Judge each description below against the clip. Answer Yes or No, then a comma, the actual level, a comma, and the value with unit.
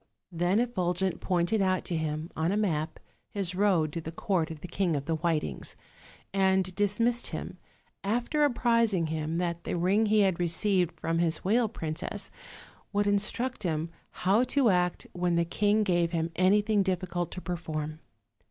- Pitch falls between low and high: Yes, medium, 180 Hz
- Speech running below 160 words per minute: No, average, 165 wpm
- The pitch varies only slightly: No, average, 3.6 semitones